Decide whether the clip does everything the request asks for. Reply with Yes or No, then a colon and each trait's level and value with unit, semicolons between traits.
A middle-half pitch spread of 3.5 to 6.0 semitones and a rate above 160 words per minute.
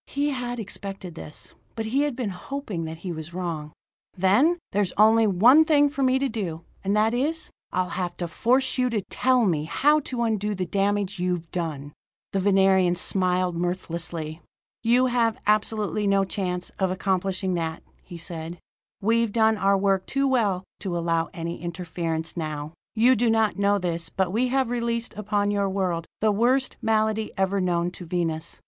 Yes: average, 4.6 semitones; average, 175 wpm